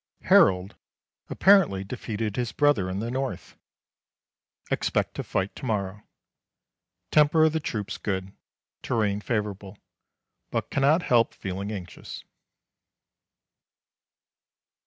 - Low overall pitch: Yes, low, 105 Hz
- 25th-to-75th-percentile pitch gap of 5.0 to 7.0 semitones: Yes, average, 5.3 semitones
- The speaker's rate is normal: No, slow, 100 wpm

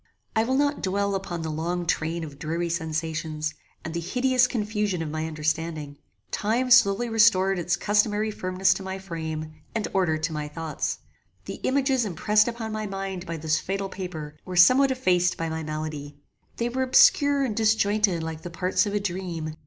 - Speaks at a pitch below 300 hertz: Yes, medium, 185 Hz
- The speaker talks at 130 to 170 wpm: No, average, 180 wpm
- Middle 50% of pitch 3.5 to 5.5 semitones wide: Yes, average, 4.9 semitones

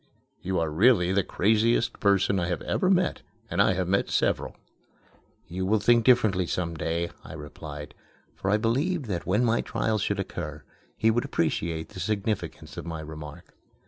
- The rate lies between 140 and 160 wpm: No, average, 175 wpm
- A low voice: Yes, very low, 95 Hz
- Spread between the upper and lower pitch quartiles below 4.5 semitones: No, average, 4.9 semitones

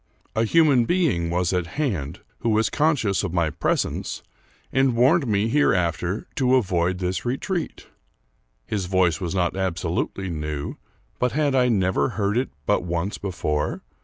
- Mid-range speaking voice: No, very low, 95 Hz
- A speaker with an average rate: Yes, average, 155 wpm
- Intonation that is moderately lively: No, wide, 6.2 semitones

